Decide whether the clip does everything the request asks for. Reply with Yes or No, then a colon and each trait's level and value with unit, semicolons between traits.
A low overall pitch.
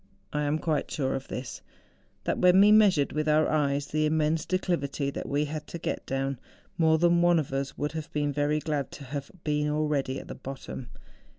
No: medium, 150 Hz